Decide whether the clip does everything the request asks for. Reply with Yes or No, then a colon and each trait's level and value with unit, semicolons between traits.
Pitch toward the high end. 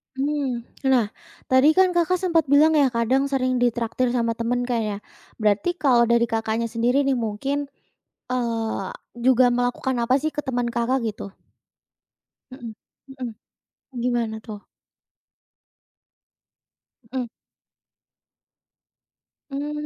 Yes: high, 245 Hz